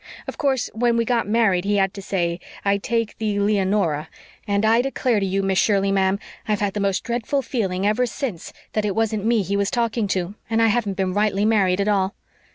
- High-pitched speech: Yes, high, 205 Hz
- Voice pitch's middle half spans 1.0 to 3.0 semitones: Yes, average, 2.7 semitones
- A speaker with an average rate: No, fast, 220 wpm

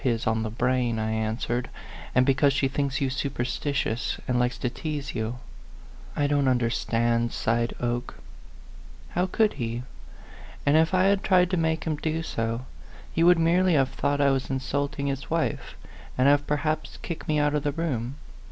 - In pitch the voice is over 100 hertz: Yes, low, 135 Hz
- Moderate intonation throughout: Yes, average, 4.2 semitones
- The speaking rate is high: No, average, 190 wpm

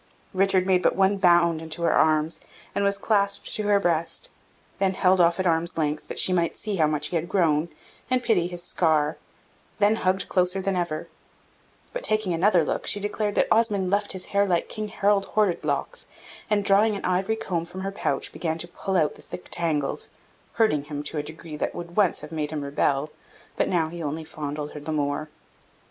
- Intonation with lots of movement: No, average, 4.0 semitones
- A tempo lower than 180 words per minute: No, fast, 205 wpm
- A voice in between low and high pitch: Yes, medium, 175 Hz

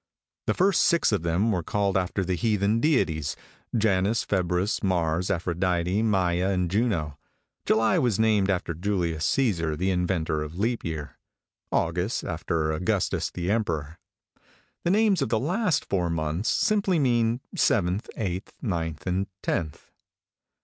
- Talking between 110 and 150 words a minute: Yes, average, 140 wpm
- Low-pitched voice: Yes, very low, 95 Hz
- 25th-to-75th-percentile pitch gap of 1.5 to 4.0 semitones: No, average, 4.7 semitones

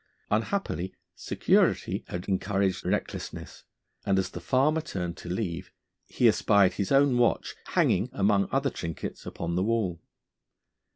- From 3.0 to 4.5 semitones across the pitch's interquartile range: No, average, 4.9 semitones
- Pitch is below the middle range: Yes, low, 100 Hz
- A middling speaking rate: No, slow, 130 wpm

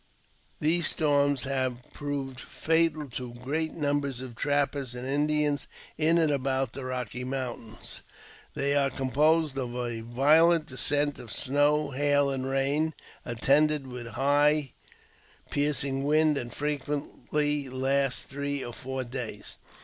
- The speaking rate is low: Yes, slow, 130 wpm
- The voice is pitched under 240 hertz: Yes, medium, 140 Hz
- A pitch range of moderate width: No, narrow, 2.3 semitones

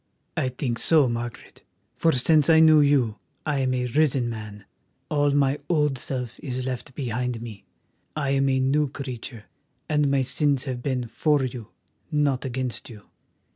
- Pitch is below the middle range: Yes, low, 130 Hz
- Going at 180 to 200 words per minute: No, average, 165 wpm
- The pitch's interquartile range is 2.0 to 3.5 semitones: Yes, average, 3.0 semitones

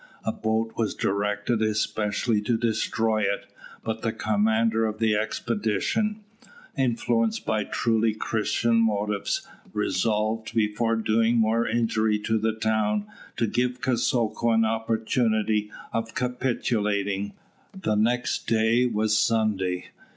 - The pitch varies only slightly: Yes, narrow, 1.4 semitones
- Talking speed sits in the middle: No, slow, 115 wpm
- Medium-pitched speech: No, low, 110 Hz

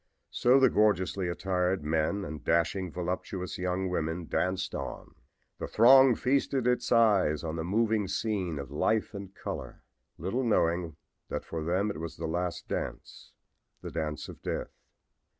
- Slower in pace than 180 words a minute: Yes, average, 150 wpm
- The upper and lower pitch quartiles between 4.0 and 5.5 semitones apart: Yes, average, 4.3 semitones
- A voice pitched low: Yes, very low, 90 Hz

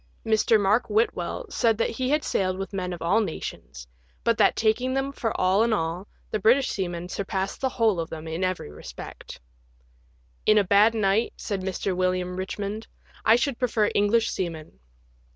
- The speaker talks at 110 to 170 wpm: No, average, 185 wpm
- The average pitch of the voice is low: No, high, 200 Hz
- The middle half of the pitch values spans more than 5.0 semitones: No, average, 3.8 semitones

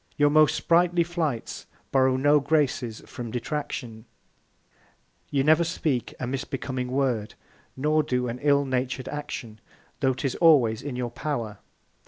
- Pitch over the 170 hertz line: No, low, 135 Hz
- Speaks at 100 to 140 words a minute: Yes, slow, 135 wpm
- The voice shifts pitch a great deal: No, average, 3.3 semitones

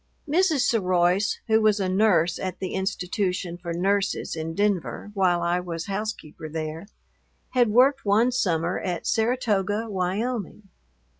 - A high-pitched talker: Yes, high, 195 Hz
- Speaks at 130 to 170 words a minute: Yes, slow, 135 wpm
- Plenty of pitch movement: No, average, 3.7 semitones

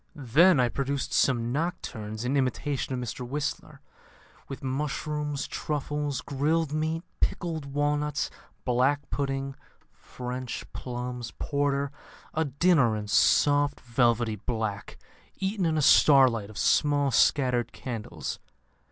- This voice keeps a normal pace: No, slow, 115 wpm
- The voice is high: No, medium, 140 Hz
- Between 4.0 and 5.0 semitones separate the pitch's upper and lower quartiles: No, average, 3.1 semitones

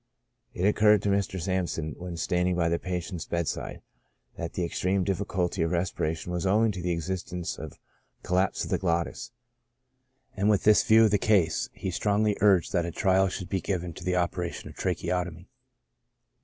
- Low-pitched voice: Yes, very low, 90 Hz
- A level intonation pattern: Yes, narrow, 2.3 semitones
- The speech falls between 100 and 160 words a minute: No, average, 185 wpm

